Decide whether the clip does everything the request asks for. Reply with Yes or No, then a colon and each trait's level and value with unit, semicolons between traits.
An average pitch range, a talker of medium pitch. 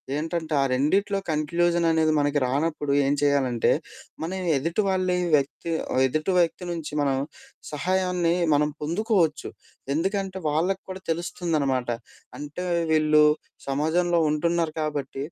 Yes: average, 3.1 semitones; medium, 160 Hz